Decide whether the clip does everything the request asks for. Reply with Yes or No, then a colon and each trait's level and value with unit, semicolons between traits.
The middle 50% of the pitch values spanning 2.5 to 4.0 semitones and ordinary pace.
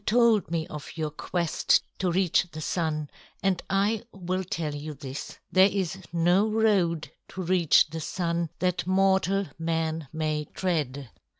Yes: average, 3.3 semitones; average, 155 wpm